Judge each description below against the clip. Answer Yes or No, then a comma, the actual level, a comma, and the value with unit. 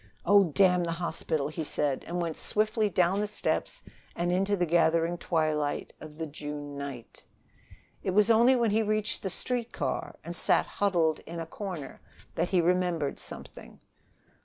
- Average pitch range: Yes, average, 4.4 semitones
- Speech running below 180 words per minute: Yes, average, 165 wpm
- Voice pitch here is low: No, medium, 175 Hz